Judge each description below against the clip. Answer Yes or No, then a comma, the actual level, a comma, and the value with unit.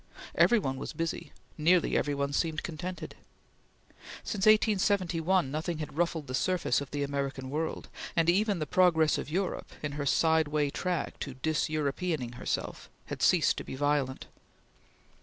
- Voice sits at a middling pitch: Yes, medium, 155 Hz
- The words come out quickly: No, average, 160 wpm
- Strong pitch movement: No, average, 3.9 semitones